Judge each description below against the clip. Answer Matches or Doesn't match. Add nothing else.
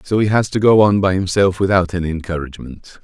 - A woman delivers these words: Doesn't match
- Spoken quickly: Matches